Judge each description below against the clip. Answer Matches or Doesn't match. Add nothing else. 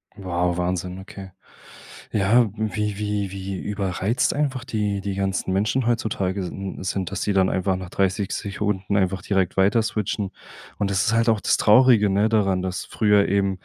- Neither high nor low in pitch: Doesn't match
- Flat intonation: Matches